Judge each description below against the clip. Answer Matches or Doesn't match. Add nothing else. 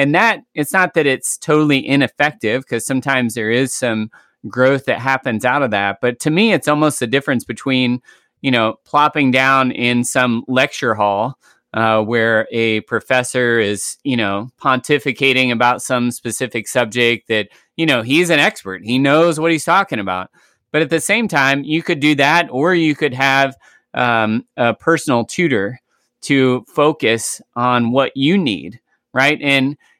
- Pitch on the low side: Matches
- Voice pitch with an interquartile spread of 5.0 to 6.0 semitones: Doesn't match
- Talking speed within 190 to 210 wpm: Doesn't match